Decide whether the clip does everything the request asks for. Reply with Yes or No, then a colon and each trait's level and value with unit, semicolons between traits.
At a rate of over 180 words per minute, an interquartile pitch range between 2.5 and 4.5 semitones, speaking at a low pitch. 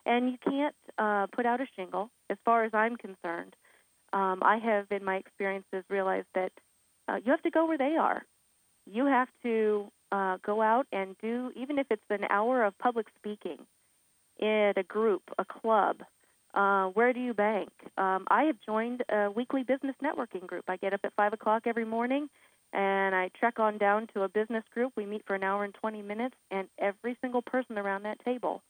No: average, 200 wpm; average, 3.8 semitones; high, 215 Hz